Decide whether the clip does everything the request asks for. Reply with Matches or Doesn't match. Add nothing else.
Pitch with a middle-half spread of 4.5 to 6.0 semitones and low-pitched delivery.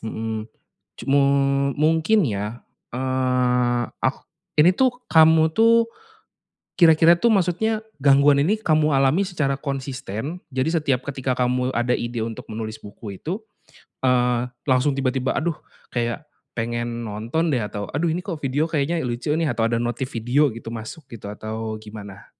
Matches